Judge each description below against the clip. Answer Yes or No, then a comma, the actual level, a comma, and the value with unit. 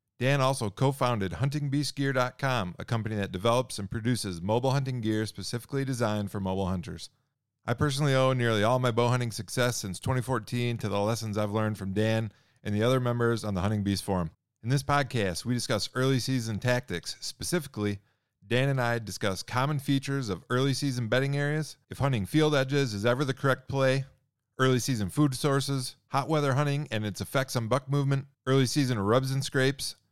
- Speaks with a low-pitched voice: Yes, low, 125 Hz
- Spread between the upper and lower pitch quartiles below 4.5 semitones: Yes, average, 4.1 semitones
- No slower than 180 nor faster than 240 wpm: Yes, average, 185 wpm